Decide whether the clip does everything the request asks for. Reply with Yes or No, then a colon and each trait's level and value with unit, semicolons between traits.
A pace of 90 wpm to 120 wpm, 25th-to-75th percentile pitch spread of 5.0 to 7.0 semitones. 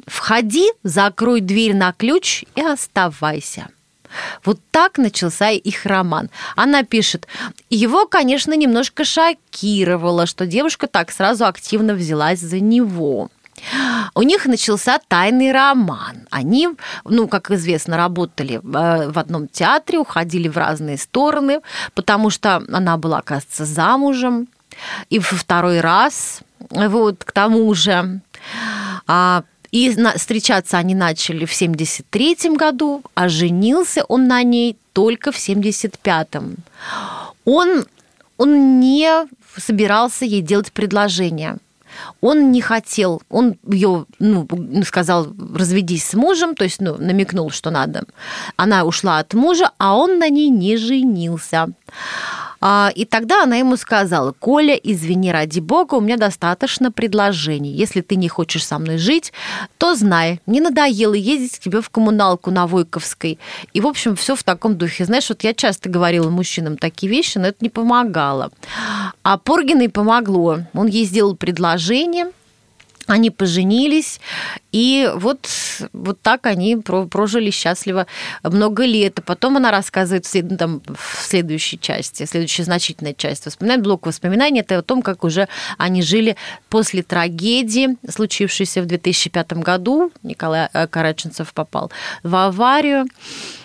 No: average, 130 wpm; wide, 5.5 semitones